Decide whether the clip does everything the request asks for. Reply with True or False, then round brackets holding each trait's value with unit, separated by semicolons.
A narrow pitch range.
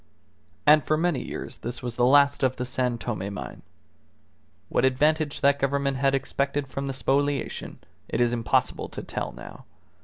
True (2.3 semitones)